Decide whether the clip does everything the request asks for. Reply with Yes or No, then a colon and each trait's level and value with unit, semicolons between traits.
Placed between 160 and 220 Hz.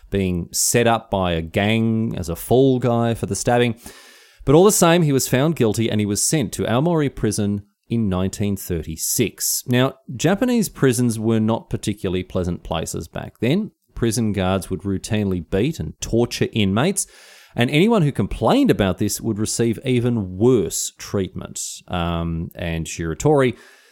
No: low, 110 Hz